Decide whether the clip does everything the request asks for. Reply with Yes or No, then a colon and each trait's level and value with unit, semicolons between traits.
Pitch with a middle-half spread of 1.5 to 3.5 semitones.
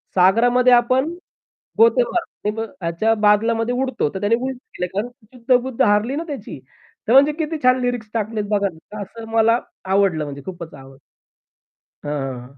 No: average, 3.9 semitones